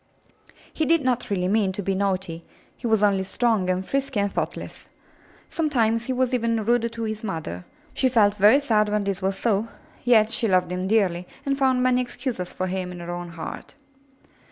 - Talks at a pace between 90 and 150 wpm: No, average, 200 wpm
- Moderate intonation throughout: Yes, average, 4.4 semitones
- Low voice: No, high, 210 Hz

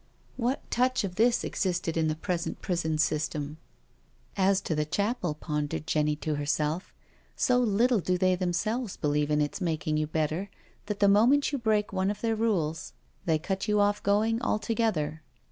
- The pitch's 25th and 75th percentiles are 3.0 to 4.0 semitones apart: No, wide, 5.6 semitones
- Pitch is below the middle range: No, medium, 185 Hz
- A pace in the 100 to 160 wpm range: No, average, 175 wpm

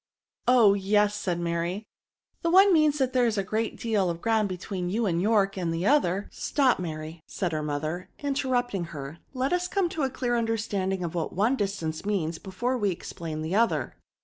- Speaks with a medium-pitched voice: No, high, 200 Hz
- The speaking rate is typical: No, fast, 215 wpm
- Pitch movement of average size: No, wide, 5.9 semitones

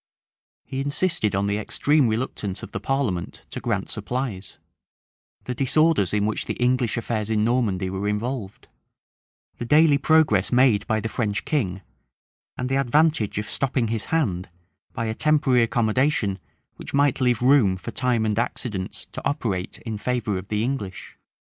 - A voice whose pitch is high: No, low, 115 Hz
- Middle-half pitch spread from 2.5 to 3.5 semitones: No, average, 4.6 semitones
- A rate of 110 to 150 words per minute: No, average, 160 wpm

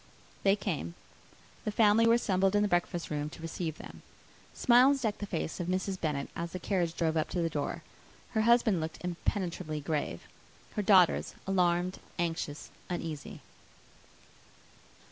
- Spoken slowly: No, average, 150 wpm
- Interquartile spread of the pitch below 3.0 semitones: No, average, 4.2 semitones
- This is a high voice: No, medium, 180 Hz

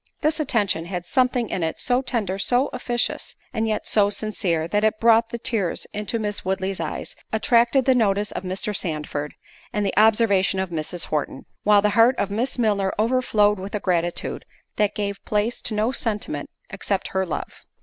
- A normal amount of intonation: Yes, average, 3.4 semitones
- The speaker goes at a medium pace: Yes, average, 180 wpm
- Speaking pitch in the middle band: No, high, 210 Hz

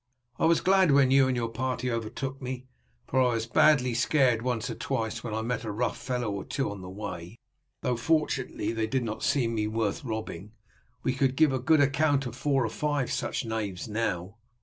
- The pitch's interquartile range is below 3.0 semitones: No, average, 3.3 semitones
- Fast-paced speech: Yes, fast, 215 wpm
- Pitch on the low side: Yes, low, 125 Hz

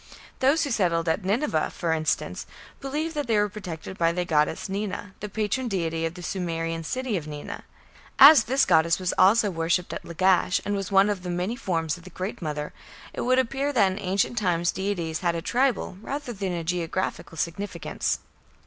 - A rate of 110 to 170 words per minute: No, average, 195 wpm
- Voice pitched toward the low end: No, medium, 185 Hz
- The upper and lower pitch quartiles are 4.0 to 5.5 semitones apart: Yes, average, 4.6 semitones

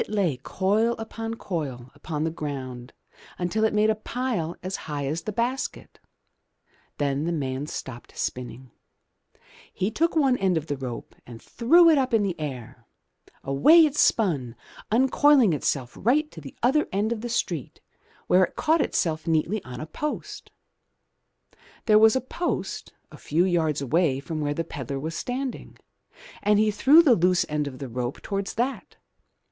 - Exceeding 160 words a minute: Yes, average, 170 wpm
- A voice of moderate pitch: Yes, medium, 180 Hz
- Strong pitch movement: Yes, wide, 8.3 semitones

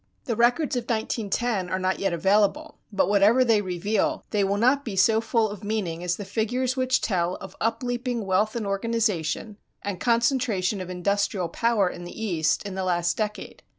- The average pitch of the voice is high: Yes, high, 205 Hz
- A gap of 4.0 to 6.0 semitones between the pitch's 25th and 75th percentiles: No, average, 3.6 semitones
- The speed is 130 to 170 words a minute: No, average, 185 wpm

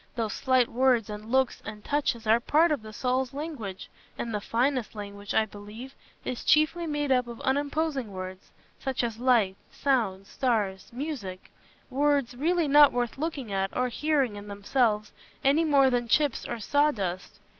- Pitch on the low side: No, high, 245 Hz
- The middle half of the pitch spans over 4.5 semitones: Yes, average, 5.1 semitones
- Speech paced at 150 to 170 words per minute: Yes, average, 160 wpm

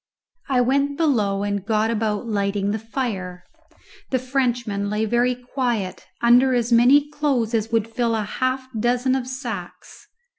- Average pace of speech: Yes, average, 150 wpm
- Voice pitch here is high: Yes, high, 235 Hz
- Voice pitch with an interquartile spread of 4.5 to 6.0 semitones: No, average, 3.4 semitones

